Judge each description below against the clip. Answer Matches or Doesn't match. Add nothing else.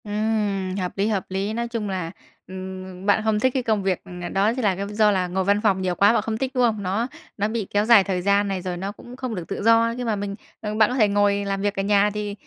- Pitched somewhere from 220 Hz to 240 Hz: Doesn't match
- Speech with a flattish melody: Matches